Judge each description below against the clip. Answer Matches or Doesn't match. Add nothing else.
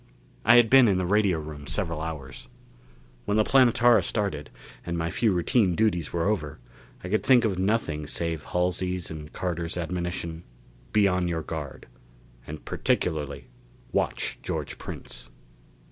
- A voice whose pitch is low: Matches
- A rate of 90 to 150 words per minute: Matches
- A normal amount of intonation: Matches